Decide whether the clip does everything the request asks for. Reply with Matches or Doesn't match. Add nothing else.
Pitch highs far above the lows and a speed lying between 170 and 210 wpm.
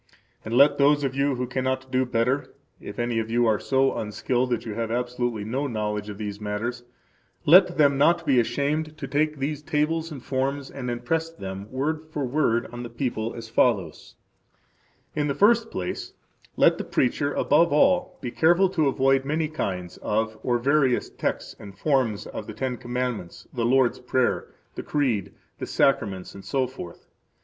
Doesn't match